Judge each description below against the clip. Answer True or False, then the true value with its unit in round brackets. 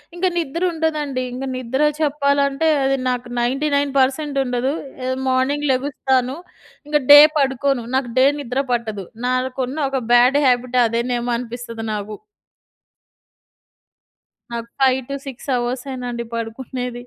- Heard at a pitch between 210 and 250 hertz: False (260 Hz)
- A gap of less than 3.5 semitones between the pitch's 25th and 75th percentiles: True (2.4 semitones)